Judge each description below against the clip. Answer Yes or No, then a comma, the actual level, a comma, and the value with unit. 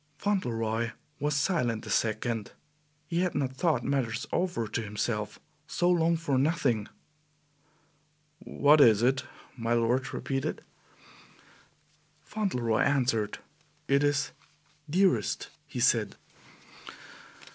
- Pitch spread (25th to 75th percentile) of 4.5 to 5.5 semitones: Yes, average, 5.0 semitones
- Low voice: Yes, low, 130 Hz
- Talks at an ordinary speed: No, slow, 105 wpm